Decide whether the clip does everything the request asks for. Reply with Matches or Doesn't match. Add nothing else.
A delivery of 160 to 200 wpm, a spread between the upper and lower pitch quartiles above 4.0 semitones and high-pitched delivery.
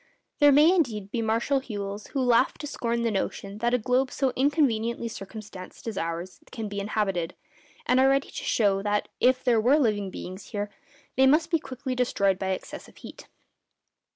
Matches